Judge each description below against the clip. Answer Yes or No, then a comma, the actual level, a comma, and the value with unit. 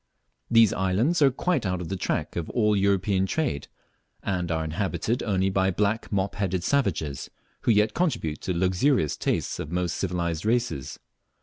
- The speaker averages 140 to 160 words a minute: No, average, 175 wpm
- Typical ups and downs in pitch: Yes, average, 4.2 semitones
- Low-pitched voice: Yes, very low, 95 Hz